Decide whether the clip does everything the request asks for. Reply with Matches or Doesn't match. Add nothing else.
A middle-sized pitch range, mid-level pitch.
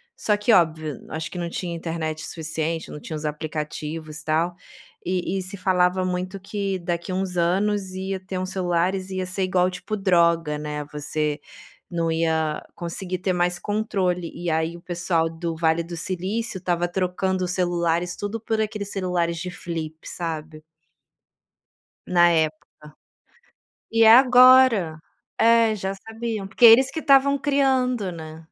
Matches